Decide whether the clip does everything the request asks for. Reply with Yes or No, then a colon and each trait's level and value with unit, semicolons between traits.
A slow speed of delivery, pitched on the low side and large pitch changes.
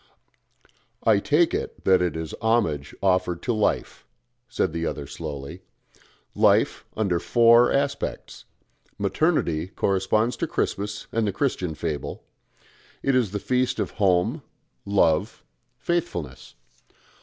Yes: slow, 120 wpm; low, 100 Hz; wide, 5.9 semitones